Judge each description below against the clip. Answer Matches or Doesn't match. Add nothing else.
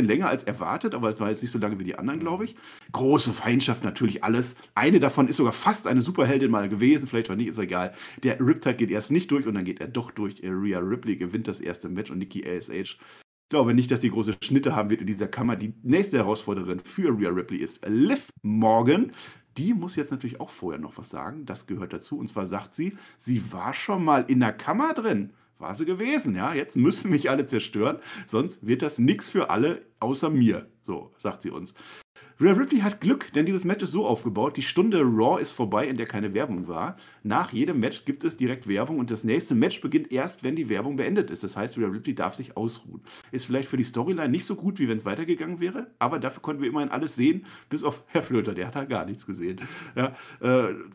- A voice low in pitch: Matches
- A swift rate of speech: Matches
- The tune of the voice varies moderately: Doesn't match